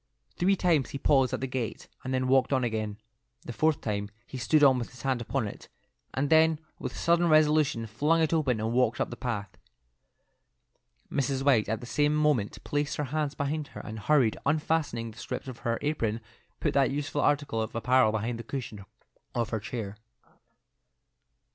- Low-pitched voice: Yes, low, 130 Hz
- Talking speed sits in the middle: Yes, average, 185 wpm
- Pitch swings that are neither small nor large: Yes, average, 4.4 semitones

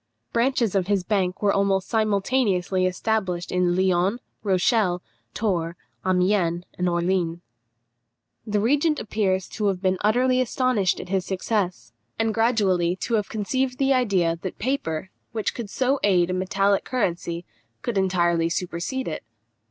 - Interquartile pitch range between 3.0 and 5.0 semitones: Yes, average, 3.7 semitones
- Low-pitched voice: No, high, 195 Hz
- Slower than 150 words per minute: Yes, average, 140 wpm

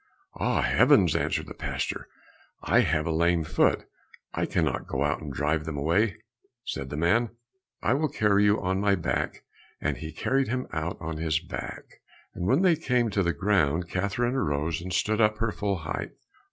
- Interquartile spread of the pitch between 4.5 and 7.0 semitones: Yes, average, 5.3 semitones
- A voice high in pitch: No, very low, 90 Hz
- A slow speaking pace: No, average, 190 wpm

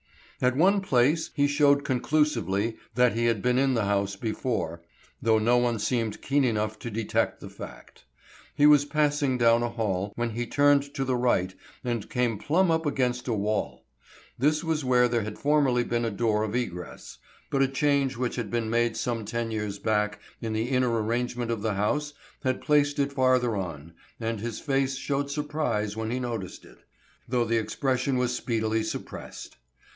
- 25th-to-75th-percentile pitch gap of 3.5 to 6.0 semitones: Yes, average, 3.9 semitones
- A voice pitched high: No, low, 120 Hz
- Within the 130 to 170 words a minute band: No, average, 185 wpm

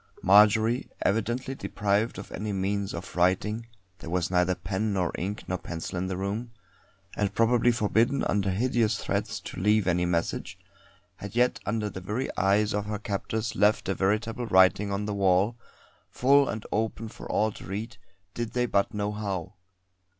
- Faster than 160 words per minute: Yes, average, 170 wpm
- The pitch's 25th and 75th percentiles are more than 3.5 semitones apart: No, average, 2.8 semitones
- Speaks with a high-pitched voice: No, low, 105 Hz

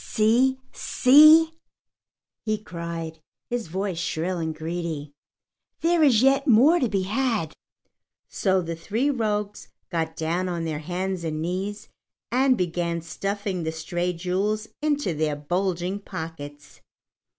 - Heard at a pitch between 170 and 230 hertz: Yes, medium, 185 Hz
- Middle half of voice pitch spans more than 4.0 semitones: Yes, average, 5.1 semitones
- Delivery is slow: Yes, slow, 130 wpm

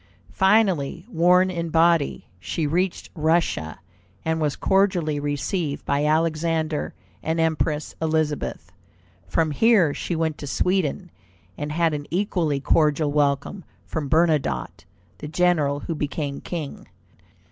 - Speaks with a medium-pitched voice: Yes, medium, 160 Hz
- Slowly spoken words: Yes, slow, 120 wpm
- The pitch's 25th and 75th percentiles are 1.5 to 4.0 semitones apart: Yes, average, 2.8 semitones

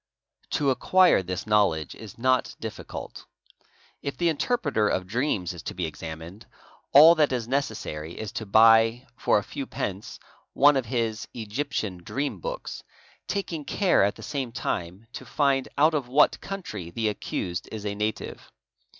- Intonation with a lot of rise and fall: Yes, wide, 6.3 semitones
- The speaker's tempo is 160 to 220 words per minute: Yes, average, 175 wpm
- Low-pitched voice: Yes, low, 115 Hz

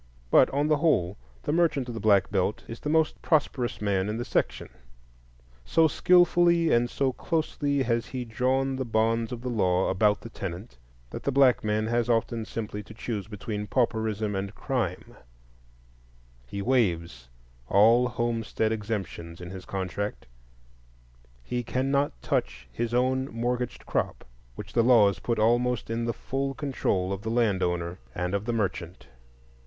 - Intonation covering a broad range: No, average, 4.2 semitones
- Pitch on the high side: No, low, 115 Hz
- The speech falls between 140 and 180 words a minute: Yes, average, 160 wpm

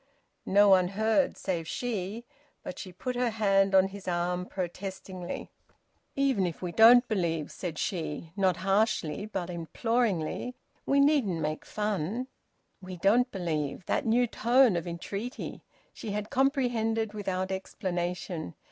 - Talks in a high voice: Yes, high, 195 Hz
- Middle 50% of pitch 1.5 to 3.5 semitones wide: No, average, 4.1 semitones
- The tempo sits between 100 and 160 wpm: Yes, average, 140 wpm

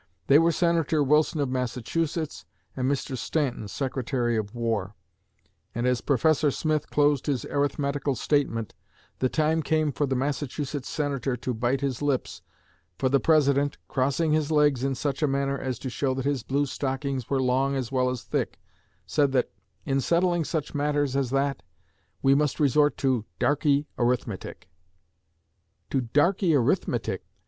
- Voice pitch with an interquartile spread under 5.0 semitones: Yes, narrow, 2.4 semitones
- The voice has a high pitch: No, medium, 140 Hz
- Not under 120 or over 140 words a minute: No, average, 155 wpm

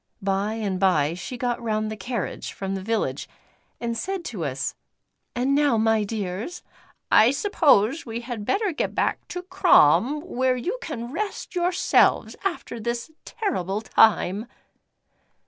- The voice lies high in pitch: Yes, high, 235 Hz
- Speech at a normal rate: Yes, average, 145 wpm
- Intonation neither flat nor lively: No, wide, 6.4 semitones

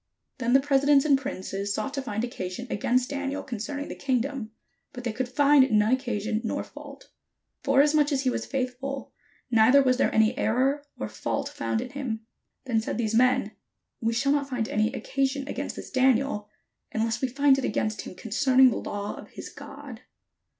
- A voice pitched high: Yes, very high, 255 Hz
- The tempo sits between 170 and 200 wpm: Yes, average, 185 wpm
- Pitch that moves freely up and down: No, average, 3.6 semitones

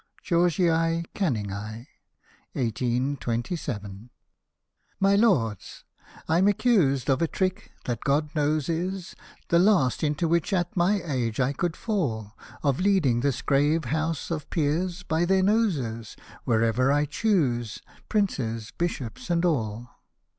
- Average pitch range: No, wide, 6.5 semitones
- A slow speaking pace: Yes, slow, 125 wpm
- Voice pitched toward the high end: No, medium, 150 Hz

